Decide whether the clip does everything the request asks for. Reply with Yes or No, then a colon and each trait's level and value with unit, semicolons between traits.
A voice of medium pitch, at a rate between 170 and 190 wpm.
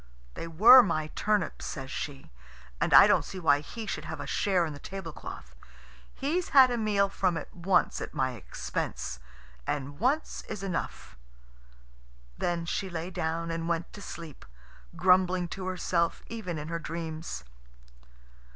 No: medium, 170 Hz; average, 155 wpm